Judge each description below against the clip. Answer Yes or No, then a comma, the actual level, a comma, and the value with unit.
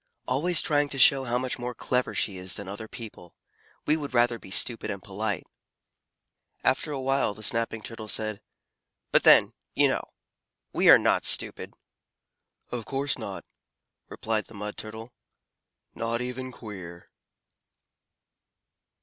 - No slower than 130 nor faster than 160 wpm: Yes, average, 140 wpm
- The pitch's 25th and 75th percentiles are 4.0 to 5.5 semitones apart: No, average, 3.5 semitones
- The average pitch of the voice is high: No, low, 115 Hz